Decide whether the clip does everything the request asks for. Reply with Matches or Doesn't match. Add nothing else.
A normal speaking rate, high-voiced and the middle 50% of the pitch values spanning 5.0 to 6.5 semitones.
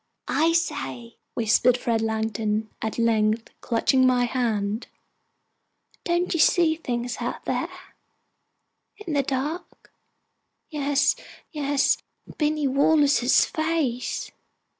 Doesn't match